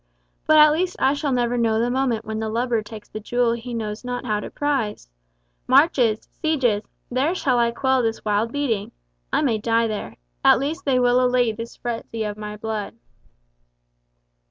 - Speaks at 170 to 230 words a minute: Yes, average, 180 wpm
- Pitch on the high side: Yes, high, 240 Hz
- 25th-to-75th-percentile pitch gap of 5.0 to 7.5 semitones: No, average, 3.2 semitones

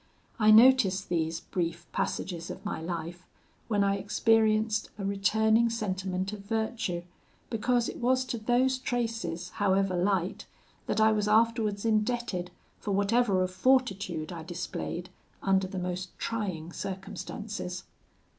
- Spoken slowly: Yes, slow, 130 wpm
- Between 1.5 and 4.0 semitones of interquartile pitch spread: Yes, average, 3.6 semitones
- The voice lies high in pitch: Yes, high, 200 Hz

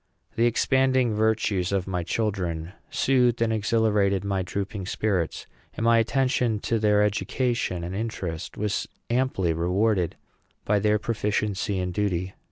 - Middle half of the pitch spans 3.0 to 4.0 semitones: Yes, average, 3.4 semitones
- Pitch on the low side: Yes, low, 105 Hz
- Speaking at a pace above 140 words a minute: No, slow, 135 wpm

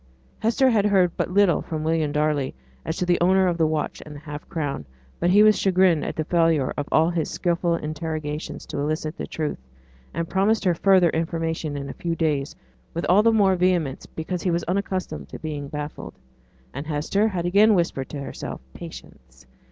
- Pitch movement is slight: No, average, 3.4 semitones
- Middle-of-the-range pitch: Yes, medium, 165 Hz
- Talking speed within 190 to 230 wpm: Yes, average, 195 wpm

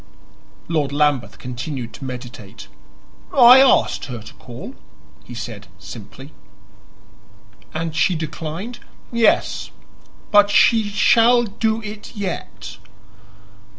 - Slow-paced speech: Yes, slow, 100 wpm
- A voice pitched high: No, medium, 160 Hz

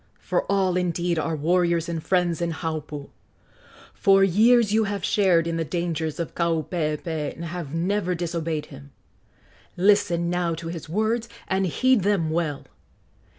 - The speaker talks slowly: No, average, 150 wpm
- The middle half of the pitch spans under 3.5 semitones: Yes, average, 2.8 semitones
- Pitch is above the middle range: No, medium, 170 Hz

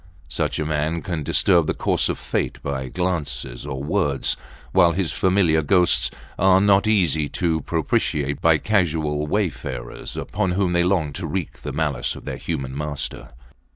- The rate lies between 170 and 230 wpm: No, average, 160 wpm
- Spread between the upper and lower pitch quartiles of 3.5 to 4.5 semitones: Yes, average, 4.0 semitones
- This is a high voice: No, very low, 80 Hz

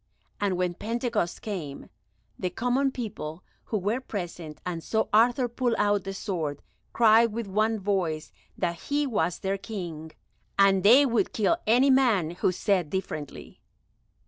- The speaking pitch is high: Yes, high, 200 Hz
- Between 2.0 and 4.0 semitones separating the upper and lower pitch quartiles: No, average, 4.8 semitones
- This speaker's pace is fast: No, average, 145 wpm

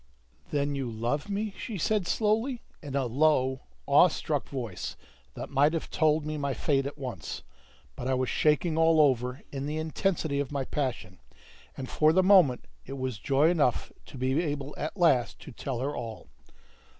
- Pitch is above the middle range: No, medium, 140 Hz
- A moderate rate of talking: Yes, average, 180 wpm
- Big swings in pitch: No, average, 3.4 semitones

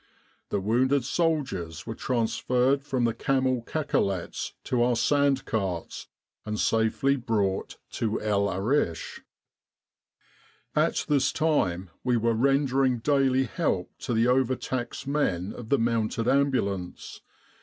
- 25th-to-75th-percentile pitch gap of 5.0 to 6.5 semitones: No, average, 4.2 semitones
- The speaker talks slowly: Yes, slow, 125 wpm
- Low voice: Yes, low, 120 Hz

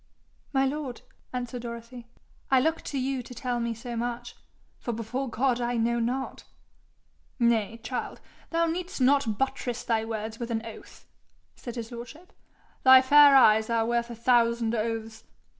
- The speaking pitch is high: Yes, high, 240 Hz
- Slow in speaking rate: No, average, 160 wpm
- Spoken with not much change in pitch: Yes, narrow, 2.2 semitones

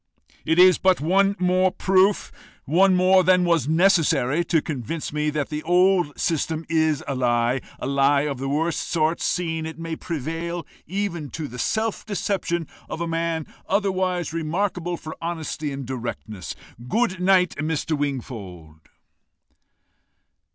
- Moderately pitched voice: Yes, medium, 165 Hz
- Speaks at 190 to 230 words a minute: No, average, 140 wpm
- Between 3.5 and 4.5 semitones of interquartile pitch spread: Yes, average, 3.9 semitones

